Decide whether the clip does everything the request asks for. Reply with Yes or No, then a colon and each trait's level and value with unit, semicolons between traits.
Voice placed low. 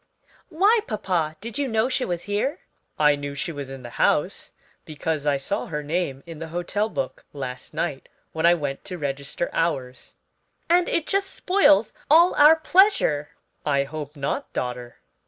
No: medium, 165 Hz